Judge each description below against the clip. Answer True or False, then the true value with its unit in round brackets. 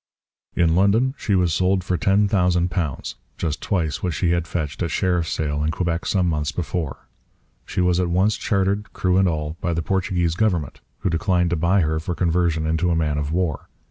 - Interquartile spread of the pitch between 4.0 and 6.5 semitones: False (2.7 semitones)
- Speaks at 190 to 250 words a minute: True (195 wpm)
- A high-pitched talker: False (85 Hz)